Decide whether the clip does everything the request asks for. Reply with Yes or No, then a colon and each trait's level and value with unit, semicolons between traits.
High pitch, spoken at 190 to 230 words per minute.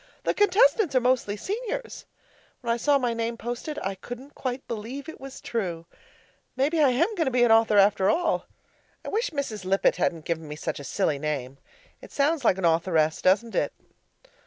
Yes: high, 235 Hz; average, 195 wpm